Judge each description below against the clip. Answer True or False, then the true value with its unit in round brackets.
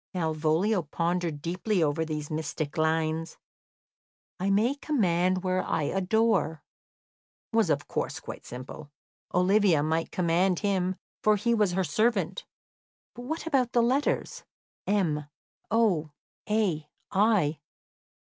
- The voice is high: False (180 Hz)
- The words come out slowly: True (120 wpm)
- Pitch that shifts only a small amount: False (5.1 semitones)